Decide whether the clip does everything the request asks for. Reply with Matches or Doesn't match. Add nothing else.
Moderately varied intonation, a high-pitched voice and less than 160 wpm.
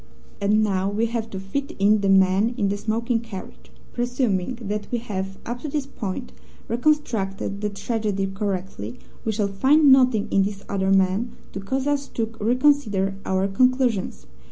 Doesn't match